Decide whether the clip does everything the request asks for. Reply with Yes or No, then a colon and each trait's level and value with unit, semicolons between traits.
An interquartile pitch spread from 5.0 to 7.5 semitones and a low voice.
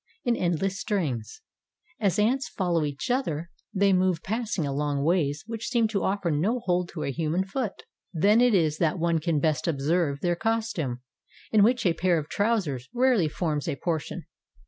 No: wide, 5.5 semitones; medium, 175 Hz